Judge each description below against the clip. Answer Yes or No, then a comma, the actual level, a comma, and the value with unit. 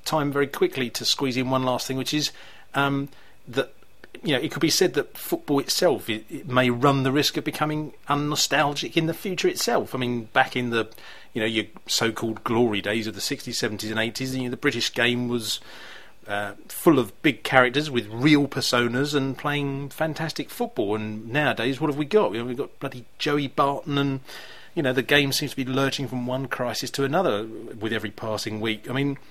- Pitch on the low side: Yes, low, 130 Hz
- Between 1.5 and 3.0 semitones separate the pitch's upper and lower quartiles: No, average, 3.5 semitones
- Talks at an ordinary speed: No, fast, 215 wpm